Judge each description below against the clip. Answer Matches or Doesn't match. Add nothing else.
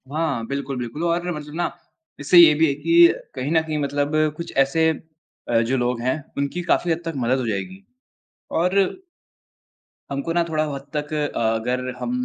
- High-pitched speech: Doesn't match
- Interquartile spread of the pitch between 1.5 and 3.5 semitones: Doesn't match